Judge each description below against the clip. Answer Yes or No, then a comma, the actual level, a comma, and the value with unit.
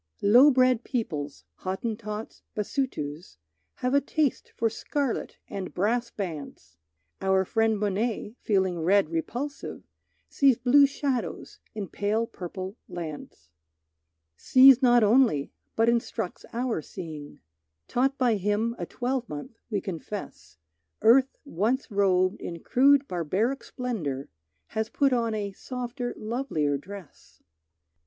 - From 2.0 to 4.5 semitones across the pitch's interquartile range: No, average, 5.3 semitones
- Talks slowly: Yes, slow, 115 wpm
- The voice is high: Yes, high, 220 Hz